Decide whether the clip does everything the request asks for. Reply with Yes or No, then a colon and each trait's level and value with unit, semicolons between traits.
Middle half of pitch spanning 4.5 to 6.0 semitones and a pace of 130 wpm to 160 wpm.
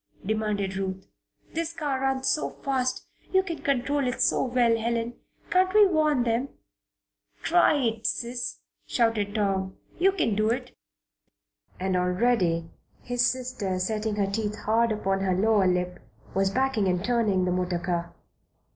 Yes: average, 5.0 semitones; average, 145 wpm